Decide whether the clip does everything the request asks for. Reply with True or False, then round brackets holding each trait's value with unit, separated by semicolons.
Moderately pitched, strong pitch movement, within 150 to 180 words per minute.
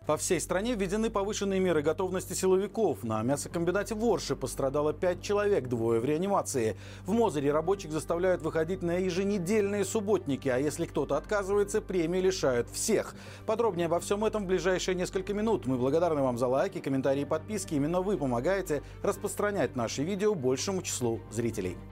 True (180 Hz; 6.6 semitones; 155 wpm)